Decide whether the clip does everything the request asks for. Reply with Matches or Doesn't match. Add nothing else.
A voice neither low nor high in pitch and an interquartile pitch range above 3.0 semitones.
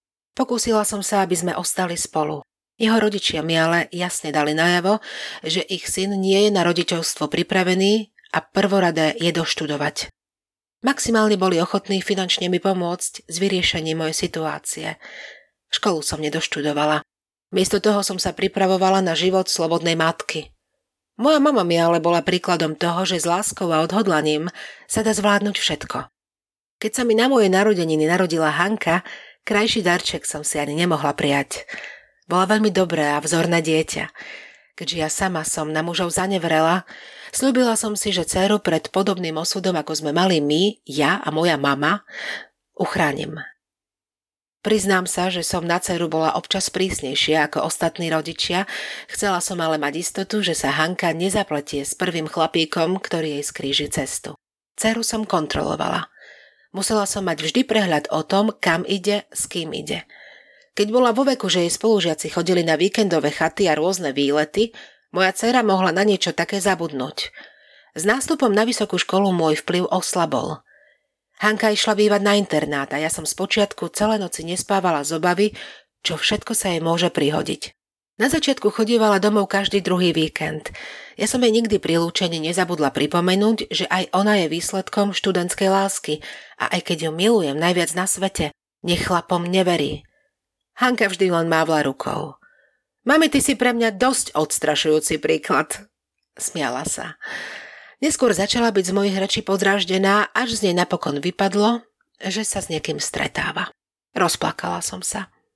Matches